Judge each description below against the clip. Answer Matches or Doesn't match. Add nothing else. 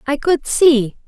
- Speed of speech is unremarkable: Matches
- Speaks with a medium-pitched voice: Doesn't match